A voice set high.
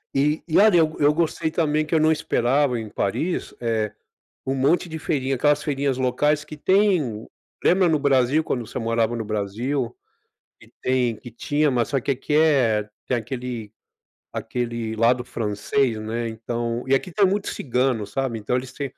No: low, 130 Hz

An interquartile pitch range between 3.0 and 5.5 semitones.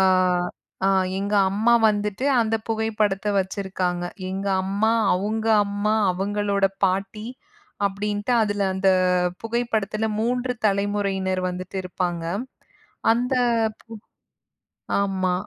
No: narrow, 2.4 semitones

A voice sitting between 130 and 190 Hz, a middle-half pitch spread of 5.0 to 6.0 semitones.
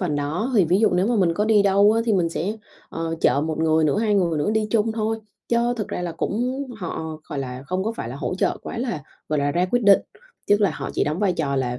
Yes: medium, 185 Hz; wide, 5.4 semitones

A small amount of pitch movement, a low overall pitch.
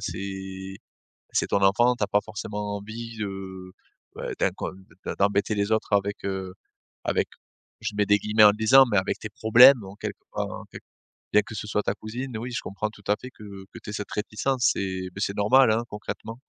Yes: narrow, 2.0 semitones; low, 105 Hz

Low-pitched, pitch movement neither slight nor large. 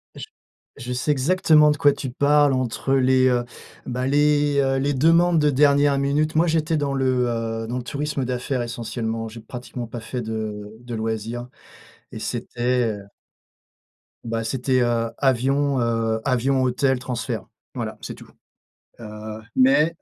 Yes: low, 130 Hz; average, 3.4 semitones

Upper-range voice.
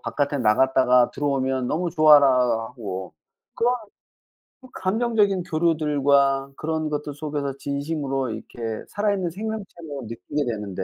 No: medium, 145 Hz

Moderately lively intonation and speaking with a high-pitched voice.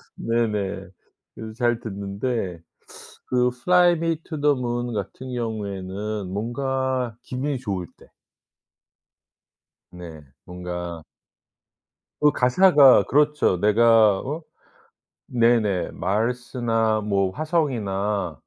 No: average, 4.6 semitones; low, 115 Hz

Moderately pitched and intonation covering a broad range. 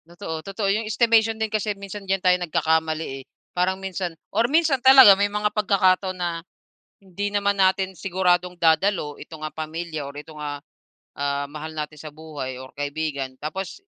No: medium, 180 Hz; average, 4.4 semitones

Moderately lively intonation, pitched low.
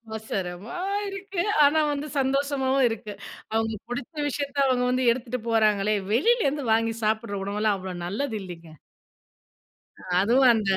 No: average, 4.7 semitones; high, 235 Hz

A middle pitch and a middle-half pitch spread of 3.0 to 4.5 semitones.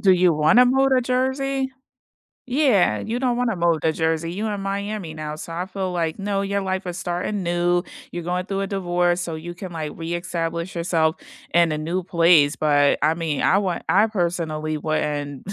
Yes: medium, 175 Hz; average, 3.5 semitones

